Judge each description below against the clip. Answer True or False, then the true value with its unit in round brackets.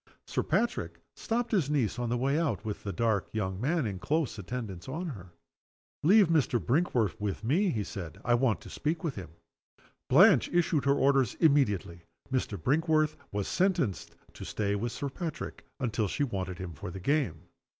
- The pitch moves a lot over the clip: True (7.4 semitones)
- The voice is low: True (125 Hz)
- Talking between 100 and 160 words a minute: False (180 wpm)